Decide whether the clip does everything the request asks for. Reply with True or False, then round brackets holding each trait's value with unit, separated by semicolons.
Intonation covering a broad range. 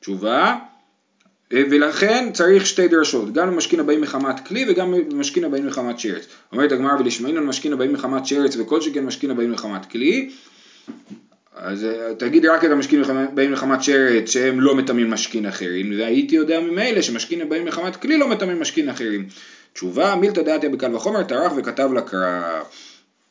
True (6.2 semitones)